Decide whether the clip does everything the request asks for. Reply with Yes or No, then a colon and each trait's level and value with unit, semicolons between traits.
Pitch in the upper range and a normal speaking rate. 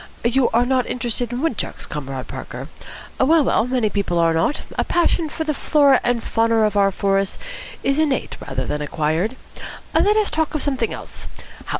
Yes: high, 240 Hz; average, 185 wpm